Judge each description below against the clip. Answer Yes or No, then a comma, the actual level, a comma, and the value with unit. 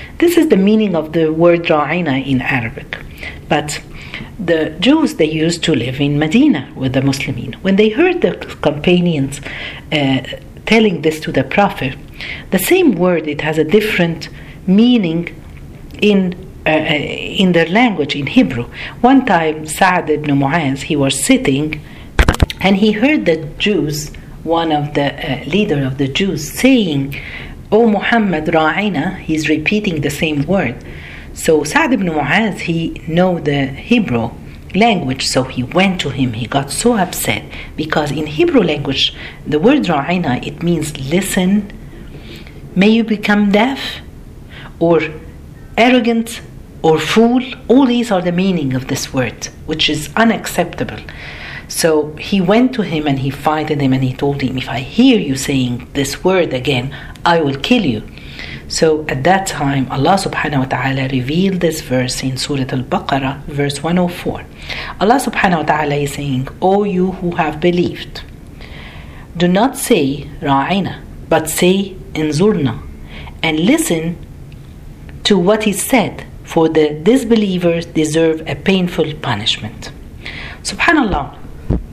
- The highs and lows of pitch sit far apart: Yes, wide, 5.8 semitones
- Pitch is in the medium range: Yes, medium, 155 Hz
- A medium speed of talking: No, fast, 145 wpm